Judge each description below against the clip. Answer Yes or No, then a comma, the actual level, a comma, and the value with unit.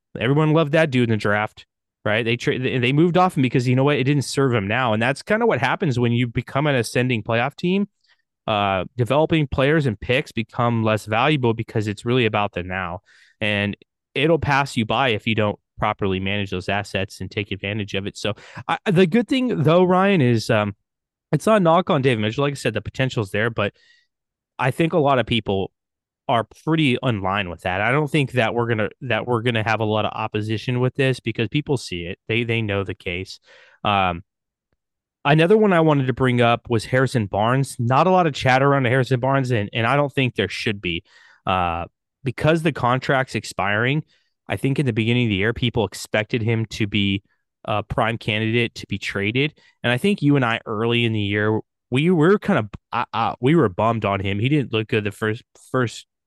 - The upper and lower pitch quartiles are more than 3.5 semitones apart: Yes, average, 4.7 semitones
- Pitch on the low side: Yes, low, 120 Hz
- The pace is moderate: No, fast, 220 wpm